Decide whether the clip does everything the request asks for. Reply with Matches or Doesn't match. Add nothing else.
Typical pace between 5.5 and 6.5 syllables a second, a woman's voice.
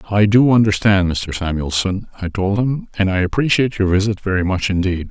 Doesn't match